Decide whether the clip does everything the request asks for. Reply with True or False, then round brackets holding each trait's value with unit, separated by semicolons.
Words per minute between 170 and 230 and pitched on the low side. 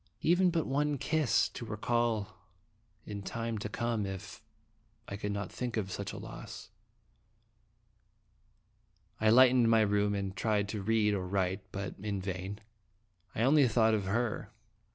False (155 wpm; 105 Hz)